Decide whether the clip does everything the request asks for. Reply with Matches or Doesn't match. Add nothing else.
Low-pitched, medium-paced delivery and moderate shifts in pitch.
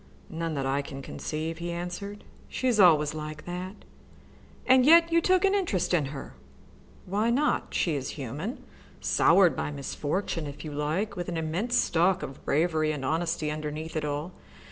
Doesn't match